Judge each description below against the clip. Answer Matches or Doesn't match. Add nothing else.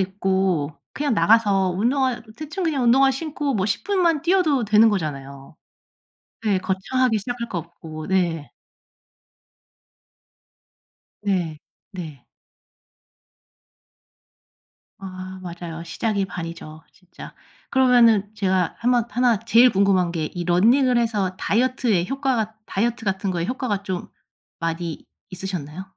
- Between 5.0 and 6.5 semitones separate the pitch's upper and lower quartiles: Matches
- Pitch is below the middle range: Doesn't match